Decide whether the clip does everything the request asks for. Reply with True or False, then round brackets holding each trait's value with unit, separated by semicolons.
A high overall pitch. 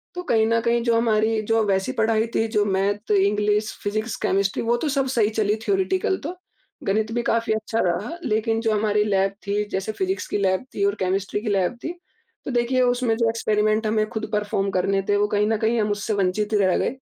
True (215 Hz)